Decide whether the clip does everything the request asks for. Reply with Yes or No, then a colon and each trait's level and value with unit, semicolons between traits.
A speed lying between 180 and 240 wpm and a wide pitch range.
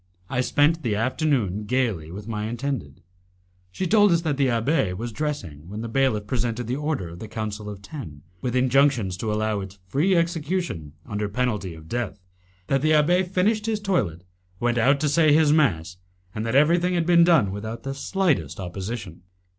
Yes: average, 185 wpm; wide, 6.8 semitones